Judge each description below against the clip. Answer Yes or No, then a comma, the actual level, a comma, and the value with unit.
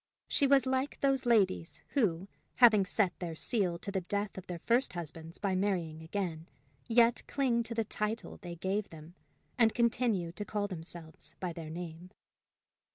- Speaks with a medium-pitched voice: No, high, 195 Hz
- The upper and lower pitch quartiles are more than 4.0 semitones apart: Yes, average, 5.2 semitones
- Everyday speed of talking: Yes, average, 165 wpm